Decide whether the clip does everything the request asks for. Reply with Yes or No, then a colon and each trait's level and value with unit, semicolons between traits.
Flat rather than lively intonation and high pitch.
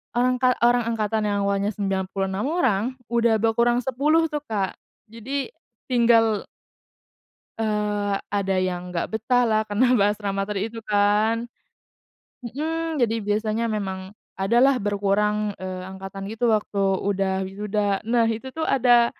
No: average, 3.2 semitones; high, 215 Hz